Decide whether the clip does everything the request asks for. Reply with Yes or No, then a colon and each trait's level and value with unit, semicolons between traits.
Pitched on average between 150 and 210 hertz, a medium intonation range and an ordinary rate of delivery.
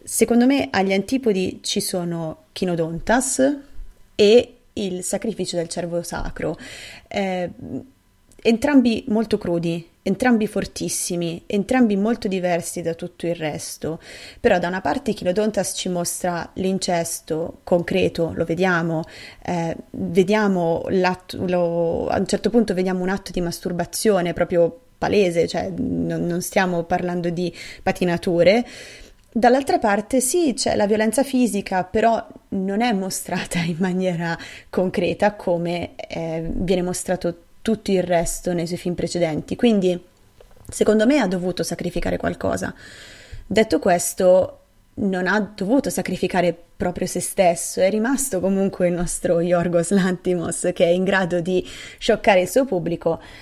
Yes: medium, 185 Hz; average, 3.4 semitones; average, 130 wpm